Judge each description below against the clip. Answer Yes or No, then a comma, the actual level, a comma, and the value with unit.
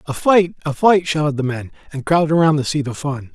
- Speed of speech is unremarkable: No, fast, 250 wpm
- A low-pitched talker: No, medium, 150 Hz